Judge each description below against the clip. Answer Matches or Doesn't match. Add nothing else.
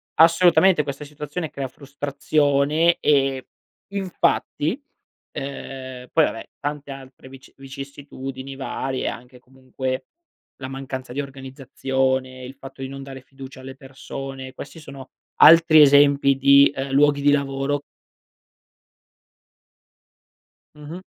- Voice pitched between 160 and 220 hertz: Doesn't match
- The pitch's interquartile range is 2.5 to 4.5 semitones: Doesn't match